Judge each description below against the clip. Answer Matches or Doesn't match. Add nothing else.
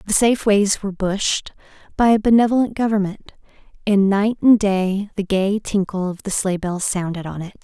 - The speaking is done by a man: Doesn't match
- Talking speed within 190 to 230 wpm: Doesn't match